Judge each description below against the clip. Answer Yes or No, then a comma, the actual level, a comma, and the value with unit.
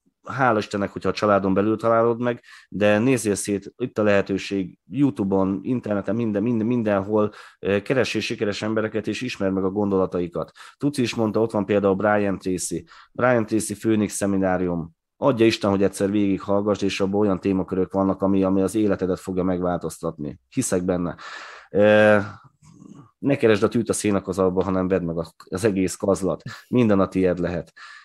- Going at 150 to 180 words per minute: Yes, fast, 155 wpm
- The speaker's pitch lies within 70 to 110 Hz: Yes, low, 100 Hz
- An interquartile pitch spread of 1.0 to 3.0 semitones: Yes, narrow, 2.6 semitones